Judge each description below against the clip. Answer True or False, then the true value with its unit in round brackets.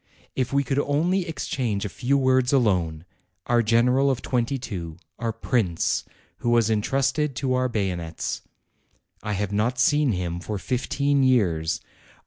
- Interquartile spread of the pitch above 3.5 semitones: True (5.0 semitones)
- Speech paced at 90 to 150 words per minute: True (145 wpm)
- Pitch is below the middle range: True (120 Hz)